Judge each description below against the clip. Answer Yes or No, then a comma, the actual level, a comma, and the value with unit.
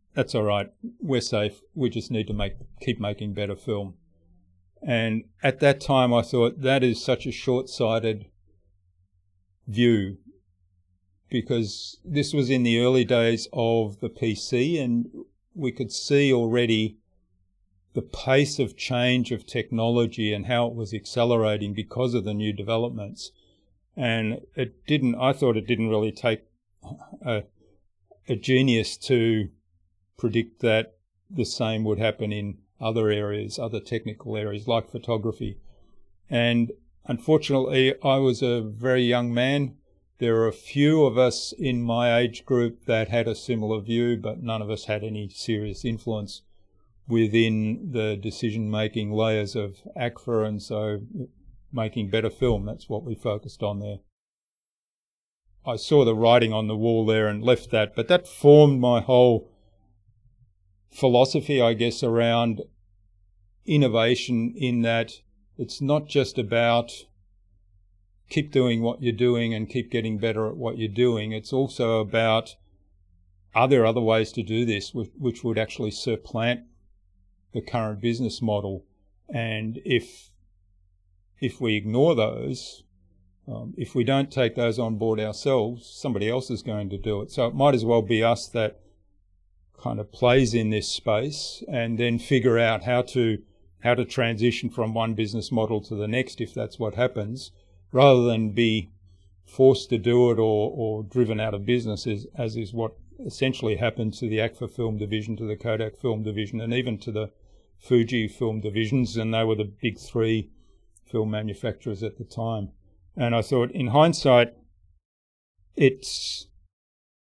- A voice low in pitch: Yes, low, 115 Hz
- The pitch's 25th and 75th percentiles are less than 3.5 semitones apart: Yes, average, 2.8 semitones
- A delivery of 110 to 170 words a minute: Yes, average, 150 wpm